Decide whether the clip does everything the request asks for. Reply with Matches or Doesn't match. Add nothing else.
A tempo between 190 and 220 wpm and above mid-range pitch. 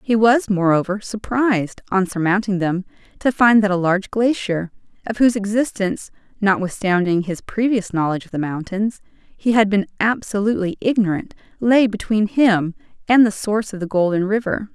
Doesn't match